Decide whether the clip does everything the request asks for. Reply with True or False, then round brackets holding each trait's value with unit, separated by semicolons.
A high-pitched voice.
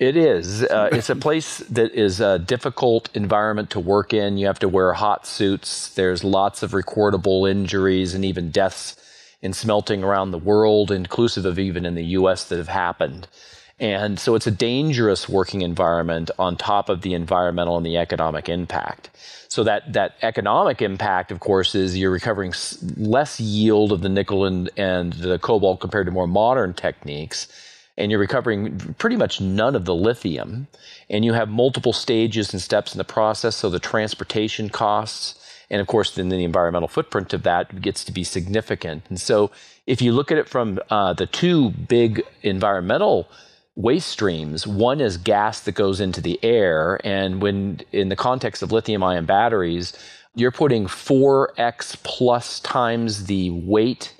False (100 Hz)